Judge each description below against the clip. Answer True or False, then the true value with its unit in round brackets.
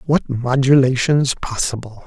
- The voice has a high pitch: False (130 Hz)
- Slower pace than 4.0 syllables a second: False (4.2 syllables/s)